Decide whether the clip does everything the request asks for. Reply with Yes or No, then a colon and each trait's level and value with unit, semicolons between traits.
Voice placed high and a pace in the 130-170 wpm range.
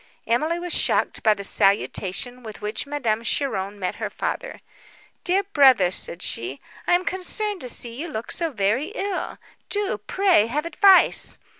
Yes: very high, 255 Hz; average, 155 wpm